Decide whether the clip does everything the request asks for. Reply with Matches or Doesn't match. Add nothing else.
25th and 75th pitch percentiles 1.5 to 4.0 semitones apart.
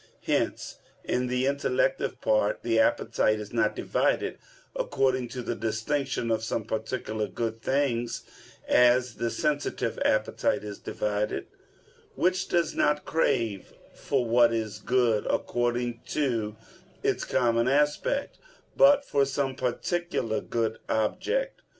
Doesn't match